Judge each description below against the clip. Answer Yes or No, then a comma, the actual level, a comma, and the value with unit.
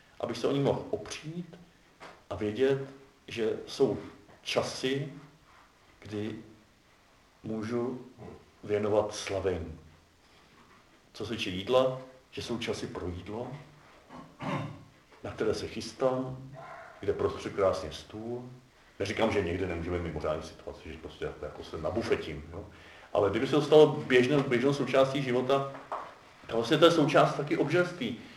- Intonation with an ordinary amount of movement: No, wide, 6.8 semitones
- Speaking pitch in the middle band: No, low, 120 Hz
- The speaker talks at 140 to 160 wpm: No, average, 125 wpm